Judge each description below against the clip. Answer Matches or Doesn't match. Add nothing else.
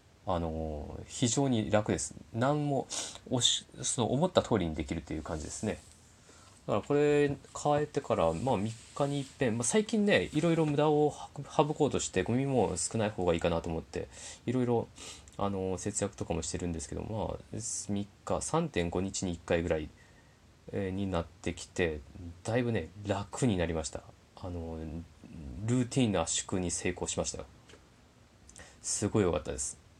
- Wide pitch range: Matches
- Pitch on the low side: Matches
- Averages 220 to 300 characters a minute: Doesn't match